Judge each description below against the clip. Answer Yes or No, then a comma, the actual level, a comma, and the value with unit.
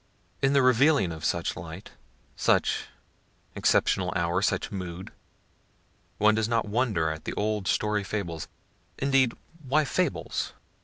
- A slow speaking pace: Yes, slow, 125 wpm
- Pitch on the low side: Yes, low, 105 Hz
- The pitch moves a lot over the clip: Yes, wide, 6.1 semitones